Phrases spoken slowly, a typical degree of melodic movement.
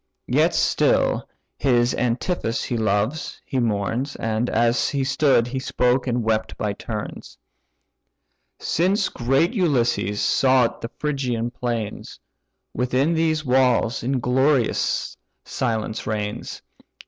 Yes: slow, 110 wpm; average, 3.1 semitones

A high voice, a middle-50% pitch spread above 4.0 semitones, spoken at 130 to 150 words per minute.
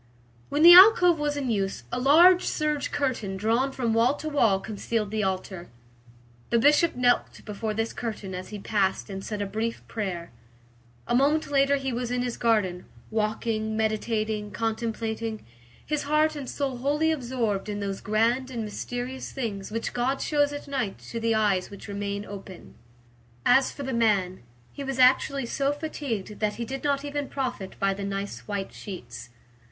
No: high, 230 Hz; average, 4.9 semitones; average, 175 wpm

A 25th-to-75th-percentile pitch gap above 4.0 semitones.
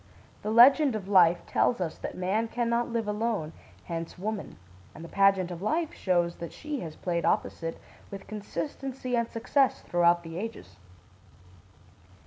Yes: average, 5.3 semitones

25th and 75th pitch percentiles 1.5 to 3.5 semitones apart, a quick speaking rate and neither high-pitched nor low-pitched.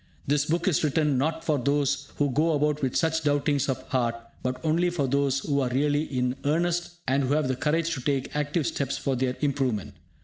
Yes: narrow, 2.6 semitones; fast, 210 wpm; medium, 145 Hz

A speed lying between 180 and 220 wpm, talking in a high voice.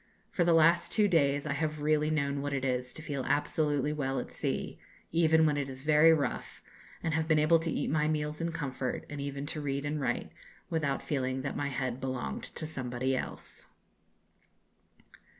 No: average, 190 wpm; medium, 145 Hz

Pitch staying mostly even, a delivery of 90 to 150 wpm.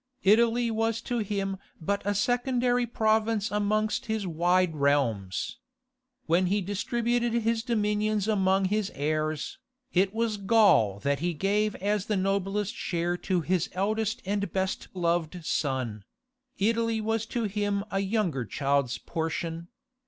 No: average, 4.2 semitones; slow, 135 wpm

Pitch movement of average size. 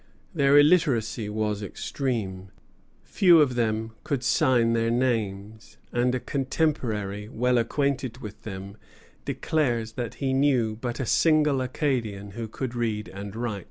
Yes: average, 3.7 semitones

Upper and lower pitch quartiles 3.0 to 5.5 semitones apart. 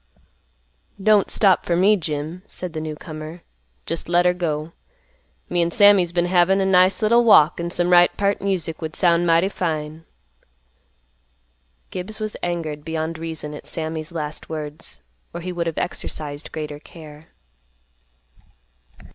No: narrow, 2.6 semitones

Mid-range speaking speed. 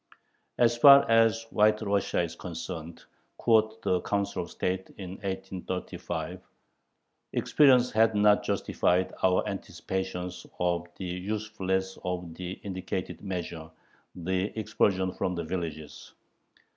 No: slow, 115 wpm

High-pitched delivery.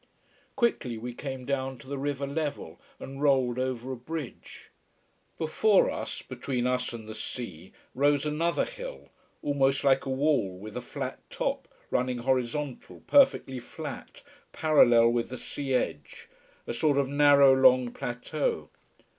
No: low, 135 Hz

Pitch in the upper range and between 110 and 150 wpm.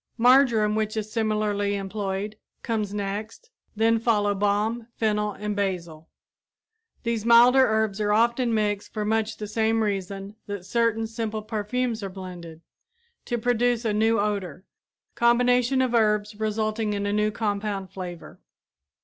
Yes: high, 215 Hz; average, 140 wpm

